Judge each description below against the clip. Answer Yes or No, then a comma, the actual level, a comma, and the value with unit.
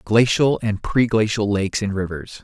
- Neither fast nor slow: Yes, average, 150 wpm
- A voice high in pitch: No, low, 105 Hz